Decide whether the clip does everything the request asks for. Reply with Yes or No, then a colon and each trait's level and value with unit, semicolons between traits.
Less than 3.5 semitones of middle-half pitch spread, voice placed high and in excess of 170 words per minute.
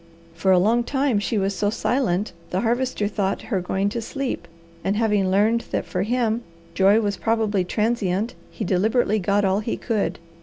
Yes: average, 3.1 semitones; high, 210 Hz; average, 180 wpm